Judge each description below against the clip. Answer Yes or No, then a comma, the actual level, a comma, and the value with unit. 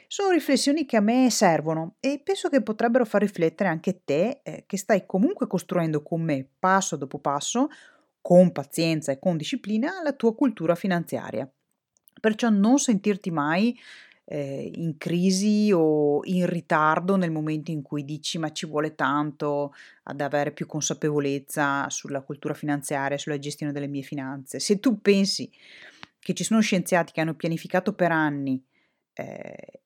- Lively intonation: Yes, wide, 6.1 semitones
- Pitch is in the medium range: Yes, medium, 170 Hz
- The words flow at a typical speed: Yes, average, 155 wpm